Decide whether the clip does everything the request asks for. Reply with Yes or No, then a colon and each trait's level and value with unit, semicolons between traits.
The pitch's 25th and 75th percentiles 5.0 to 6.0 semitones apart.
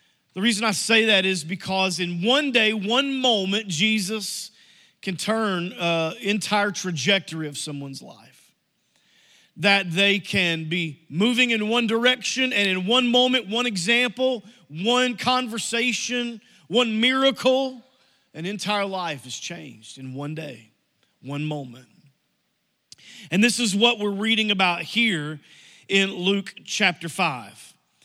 Yes: average, 5.3 semitones